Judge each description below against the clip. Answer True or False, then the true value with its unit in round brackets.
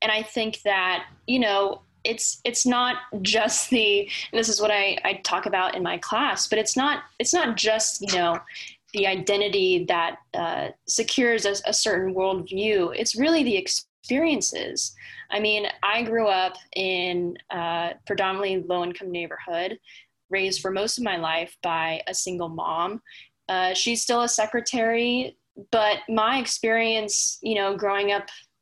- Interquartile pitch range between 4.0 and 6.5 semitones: False (3.4 semitones)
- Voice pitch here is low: False (210 Hz)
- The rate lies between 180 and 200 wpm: False (160 wpm)